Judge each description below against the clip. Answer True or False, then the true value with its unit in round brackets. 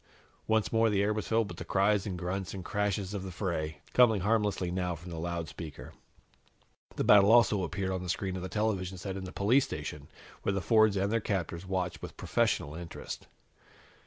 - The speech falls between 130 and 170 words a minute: False (200 wpm)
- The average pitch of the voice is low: True (95 Hz)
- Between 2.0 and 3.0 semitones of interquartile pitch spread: True (2.7 semitones)